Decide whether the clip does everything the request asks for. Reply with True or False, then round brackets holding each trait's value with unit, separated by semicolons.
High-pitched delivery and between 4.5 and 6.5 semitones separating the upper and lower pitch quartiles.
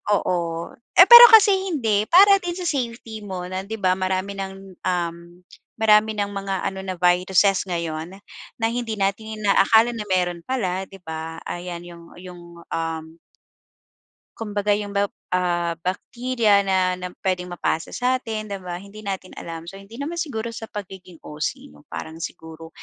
False (195 Hz; 3.8 semitones)